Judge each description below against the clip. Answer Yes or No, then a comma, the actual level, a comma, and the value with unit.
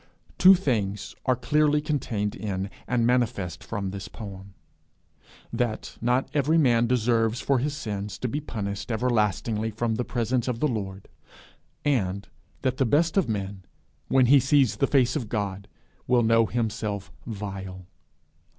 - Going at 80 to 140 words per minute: No, average, 150 wpm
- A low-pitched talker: Yes, low, 115 Hz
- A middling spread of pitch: Yes, average, 4.1 semitones